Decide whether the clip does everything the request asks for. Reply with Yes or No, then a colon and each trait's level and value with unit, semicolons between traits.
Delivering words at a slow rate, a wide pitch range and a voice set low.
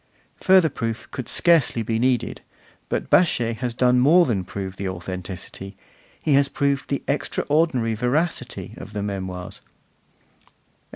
Yes: slow, 130 wpm; wide, 6.2 semitones; low, 120 Hz